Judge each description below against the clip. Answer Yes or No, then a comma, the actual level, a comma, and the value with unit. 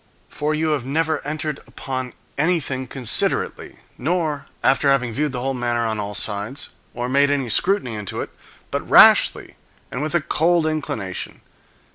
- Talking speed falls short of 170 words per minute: Yes, average, 155 wpm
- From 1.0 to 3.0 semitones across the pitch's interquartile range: No, average, 4.0 semitones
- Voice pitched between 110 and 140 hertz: Yes, low, 135 Hz